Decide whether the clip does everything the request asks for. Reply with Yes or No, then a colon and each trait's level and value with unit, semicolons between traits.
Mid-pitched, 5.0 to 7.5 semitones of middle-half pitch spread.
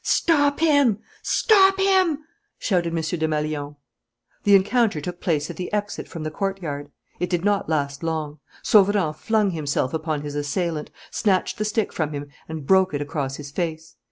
Yes: medium, 170 Hz; average, 5.3 semitones